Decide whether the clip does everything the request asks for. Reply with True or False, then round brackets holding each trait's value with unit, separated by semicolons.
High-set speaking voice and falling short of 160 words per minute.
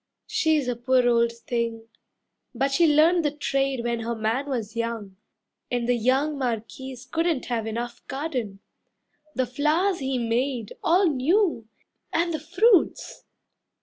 True (255 Hz; 140 wpm)